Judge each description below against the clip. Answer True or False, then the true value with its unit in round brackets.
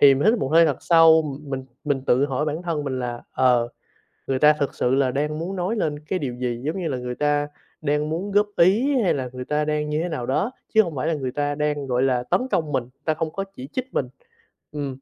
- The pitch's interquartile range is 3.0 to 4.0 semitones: True (3.7 semitones)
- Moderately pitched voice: True (150 Hz)